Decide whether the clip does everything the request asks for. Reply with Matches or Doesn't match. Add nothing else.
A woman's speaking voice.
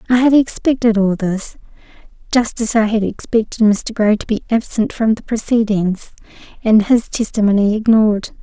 Matches